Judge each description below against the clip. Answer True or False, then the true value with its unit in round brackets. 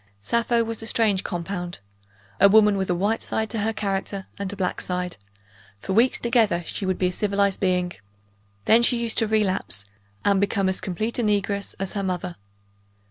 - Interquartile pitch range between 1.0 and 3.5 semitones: True (2.9 semitones)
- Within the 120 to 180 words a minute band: False (190 wpm)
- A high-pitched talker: True (200 Hz)